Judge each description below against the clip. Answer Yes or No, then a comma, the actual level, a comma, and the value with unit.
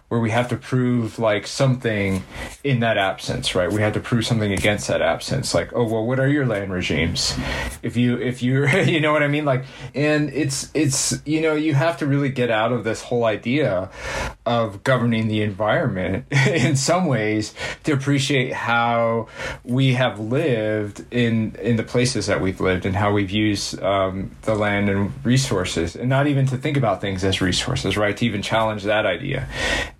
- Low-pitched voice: Yes, low, 115 Hz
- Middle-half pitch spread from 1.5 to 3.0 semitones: No, average, 4.2 semitones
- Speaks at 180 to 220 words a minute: Yes, average, 190 wpm